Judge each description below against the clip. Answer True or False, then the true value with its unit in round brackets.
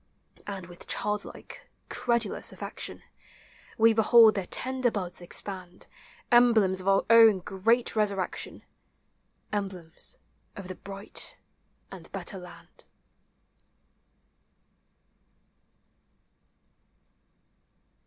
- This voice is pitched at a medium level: False (200 Hz)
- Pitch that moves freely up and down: False (3.3 semitones)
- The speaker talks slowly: True (85 wpm)